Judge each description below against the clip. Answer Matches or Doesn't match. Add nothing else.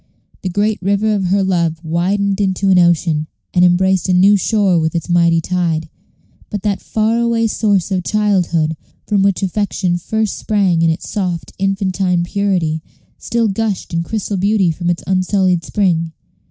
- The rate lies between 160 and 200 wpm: Matches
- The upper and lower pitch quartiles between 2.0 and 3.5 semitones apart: Matches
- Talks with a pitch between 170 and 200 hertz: Matches